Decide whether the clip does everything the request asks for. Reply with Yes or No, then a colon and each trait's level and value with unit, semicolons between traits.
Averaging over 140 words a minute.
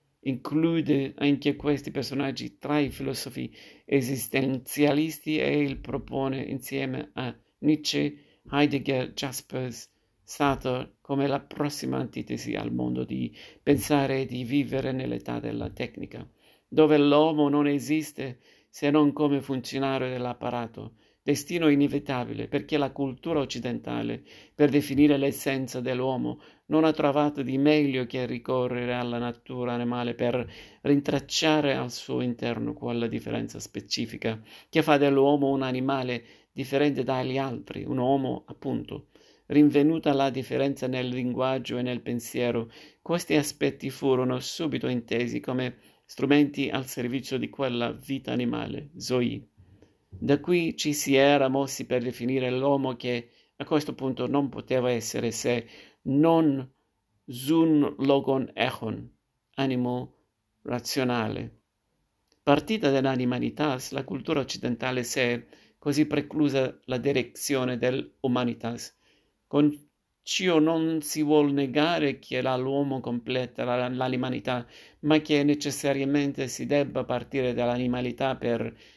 No: slow, 115 wpm